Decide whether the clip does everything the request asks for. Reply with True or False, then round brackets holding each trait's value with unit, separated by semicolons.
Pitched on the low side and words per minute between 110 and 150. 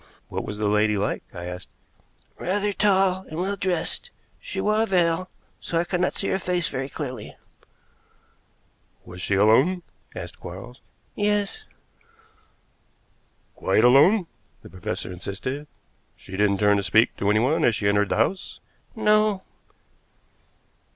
False (145 Hz; 140 wpm)